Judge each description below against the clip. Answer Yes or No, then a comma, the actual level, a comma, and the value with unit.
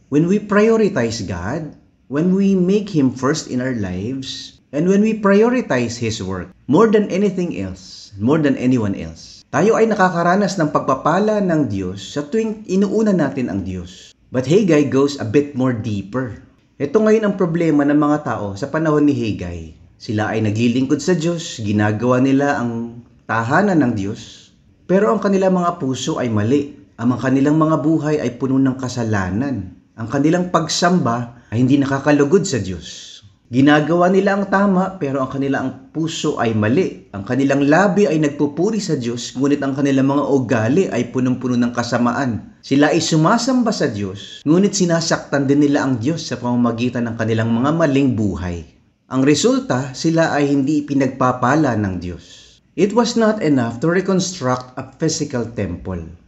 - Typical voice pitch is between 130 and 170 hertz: Yes, low, 135 Hz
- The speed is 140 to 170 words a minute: Yes, average, 160 wpm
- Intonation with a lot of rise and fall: Yes, wide, 6.0 semitones